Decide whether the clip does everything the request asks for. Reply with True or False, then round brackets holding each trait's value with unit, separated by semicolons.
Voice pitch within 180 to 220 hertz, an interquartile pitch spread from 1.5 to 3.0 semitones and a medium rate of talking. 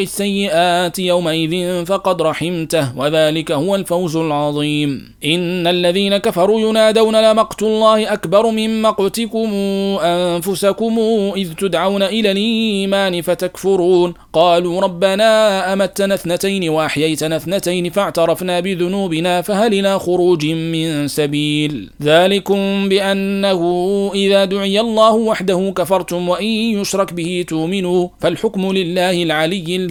True (190 Hz; 2.4 semitones; 100 wpm)